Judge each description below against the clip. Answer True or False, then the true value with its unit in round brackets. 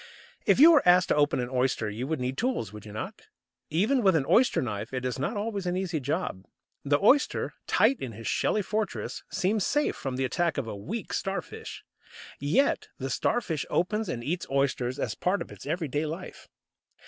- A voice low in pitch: False (155 Hz)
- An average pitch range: False (7.7 semitones)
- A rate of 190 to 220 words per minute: True (195 wpm)